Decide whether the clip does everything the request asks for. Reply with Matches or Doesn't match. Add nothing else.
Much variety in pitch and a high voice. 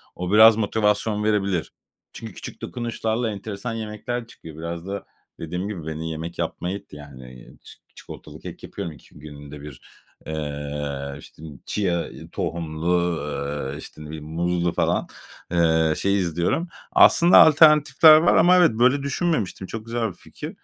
Doesn't match